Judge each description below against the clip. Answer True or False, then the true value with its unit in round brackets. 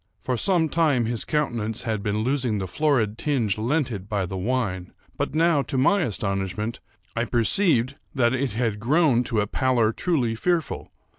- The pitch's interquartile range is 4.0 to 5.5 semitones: True (5.0 semitones)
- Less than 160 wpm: False (170 wpm)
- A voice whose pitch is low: True (120 Hz)